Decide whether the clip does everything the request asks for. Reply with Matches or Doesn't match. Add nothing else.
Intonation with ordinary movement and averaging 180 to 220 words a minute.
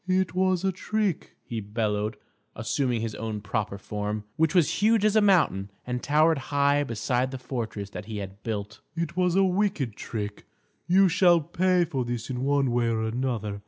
Doesn't match